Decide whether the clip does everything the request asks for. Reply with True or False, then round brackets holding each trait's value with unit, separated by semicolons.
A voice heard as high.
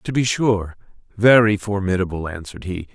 False (100 Hz)